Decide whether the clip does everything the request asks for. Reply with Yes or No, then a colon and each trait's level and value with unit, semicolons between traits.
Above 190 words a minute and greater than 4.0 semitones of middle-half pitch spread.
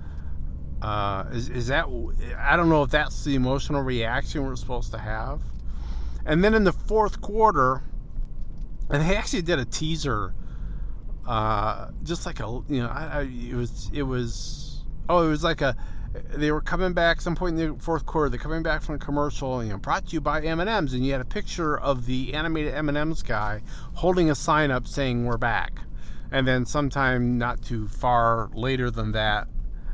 Yes: average, 200 wpm; wide, 5.4 semitones